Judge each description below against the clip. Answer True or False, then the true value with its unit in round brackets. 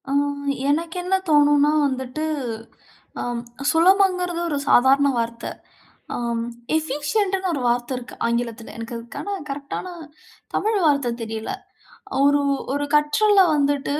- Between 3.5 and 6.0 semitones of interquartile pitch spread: True (5.4 semitones)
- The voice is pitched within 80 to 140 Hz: False (285 Hz)